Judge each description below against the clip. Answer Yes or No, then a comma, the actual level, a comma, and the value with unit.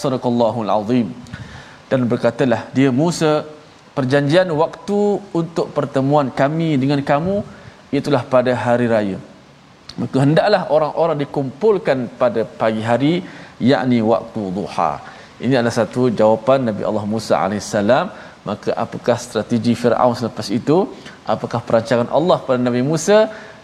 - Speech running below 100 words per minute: No, average, 120 wpm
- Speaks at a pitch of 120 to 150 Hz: Yes, low, 135 Hz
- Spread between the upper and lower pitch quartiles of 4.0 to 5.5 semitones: Yes, average, 4.4 semitones